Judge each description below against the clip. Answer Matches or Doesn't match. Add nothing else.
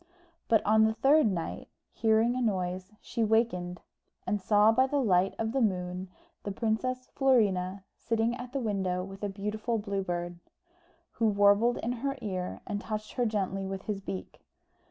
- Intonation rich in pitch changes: Doesn't match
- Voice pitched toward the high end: Matches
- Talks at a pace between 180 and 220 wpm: Doesn't match